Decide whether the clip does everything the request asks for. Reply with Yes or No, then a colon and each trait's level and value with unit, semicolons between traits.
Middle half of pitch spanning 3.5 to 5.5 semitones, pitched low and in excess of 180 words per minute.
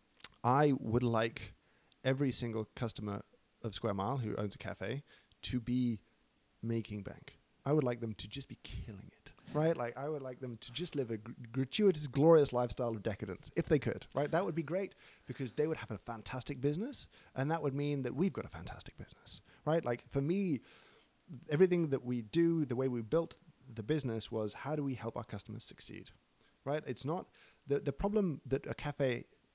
Yes: average, 4.6 semitones; low, 130 Hz; average, 200 wpm